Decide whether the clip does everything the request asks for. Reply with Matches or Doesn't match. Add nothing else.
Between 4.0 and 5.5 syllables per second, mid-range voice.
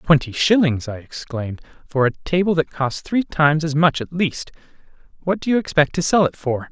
Matches